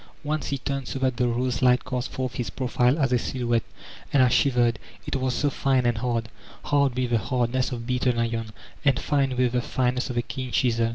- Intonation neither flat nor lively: No, narrow, 1.7 semitones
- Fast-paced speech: Yes, fast, 220 wpm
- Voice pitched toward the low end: Yes, low, 125 Hz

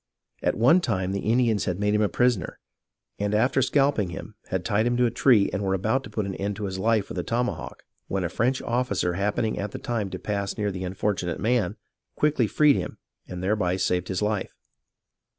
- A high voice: No, low, 105 Hz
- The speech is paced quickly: Yes, fast, 215 wpm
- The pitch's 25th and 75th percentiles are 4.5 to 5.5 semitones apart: No, average, 3.9 semitones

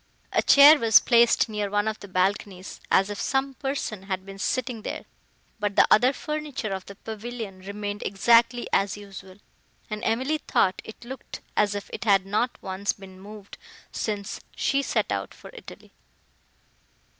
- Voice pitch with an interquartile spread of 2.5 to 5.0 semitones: Yes, average, 3.5 semitones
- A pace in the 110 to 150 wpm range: No, average, 165 wpm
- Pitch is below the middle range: No, high, 210 Hz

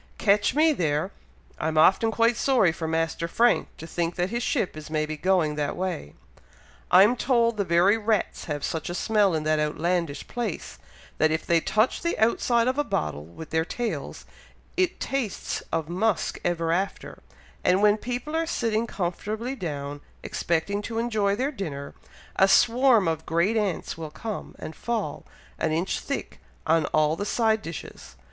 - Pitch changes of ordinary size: No, wide, 6.0 semitones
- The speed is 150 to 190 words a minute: Yes, average, 170 wpm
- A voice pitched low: No, medium, 185 Hz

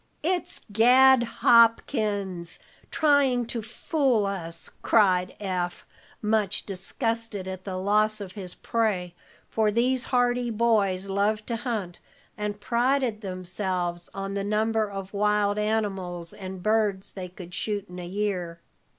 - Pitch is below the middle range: No, high, 210 Hz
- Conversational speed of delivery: No, slow, 130 wpm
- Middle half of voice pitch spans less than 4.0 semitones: Yes, average, 3.4 semitones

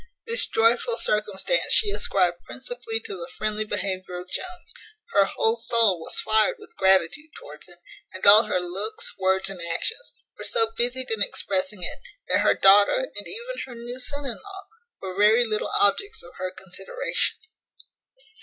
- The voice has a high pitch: Yes, high, 215 Hz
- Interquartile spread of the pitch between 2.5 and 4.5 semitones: No, wide, 5.4 semitones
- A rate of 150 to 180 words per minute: Yes, average, 165 wpm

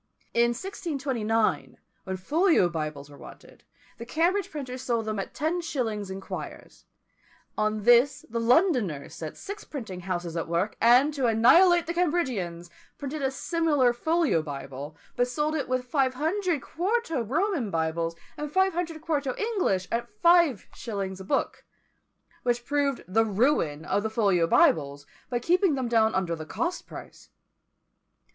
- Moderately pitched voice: No, high, 245 Hz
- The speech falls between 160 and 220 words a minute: No, average, 150 wpm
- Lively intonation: Yes, wide, 8.6 semitones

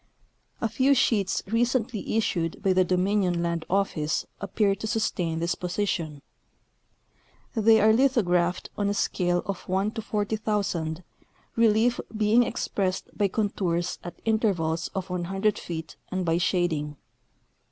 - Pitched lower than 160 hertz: No, high, 195 Hz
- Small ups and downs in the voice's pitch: No, average, 3.8 semitones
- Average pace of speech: No, slow, 130 wpm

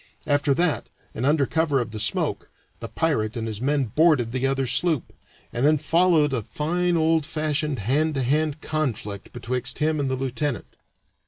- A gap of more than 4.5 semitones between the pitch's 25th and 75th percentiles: No, average, 3.8 semitones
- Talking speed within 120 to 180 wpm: Yes, average, 175 wpm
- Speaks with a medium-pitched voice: Yes, medium, 145 Hz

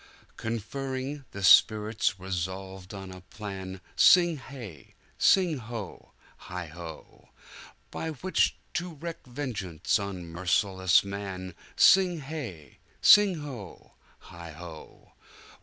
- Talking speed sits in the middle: No, slow, 90 wpm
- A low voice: Yes, low, 100 Hz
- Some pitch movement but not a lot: No, wide, 7.0 semitones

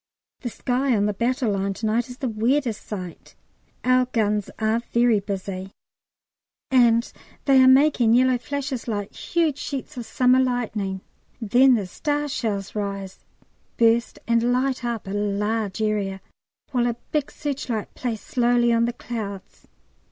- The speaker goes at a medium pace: Yes, average, 150 wpm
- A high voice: Yes, high, 235 Hz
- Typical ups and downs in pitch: Yes, average, 3.5 semitones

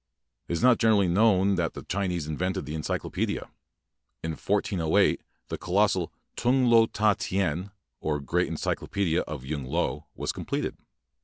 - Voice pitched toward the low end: Yes, very low, 90 Hz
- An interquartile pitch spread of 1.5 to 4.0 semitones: No, average, 4.4 semitones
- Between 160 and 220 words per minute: No, average, 145 wpm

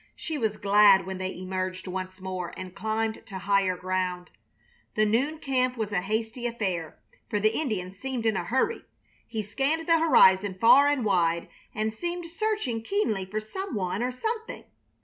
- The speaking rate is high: No, average, 170 wpm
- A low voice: No, high, 215 Hz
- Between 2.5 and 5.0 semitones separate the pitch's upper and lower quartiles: No, wide, 5.6 semitones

